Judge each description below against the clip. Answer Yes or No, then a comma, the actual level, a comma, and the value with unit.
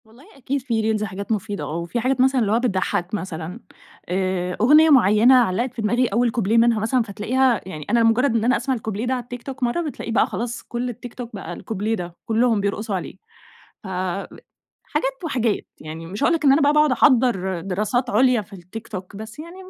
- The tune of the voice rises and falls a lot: No, average, 4.0 semitones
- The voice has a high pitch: Yes, high, 225 Hz